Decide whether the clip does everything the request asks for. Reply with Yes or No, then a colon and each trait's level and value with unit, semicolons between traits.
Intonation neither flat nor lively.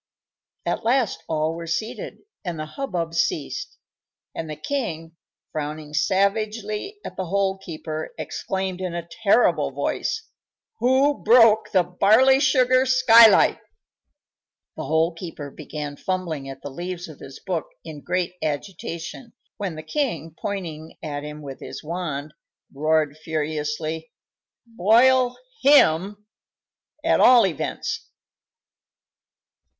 No: wide, 6.0 semitones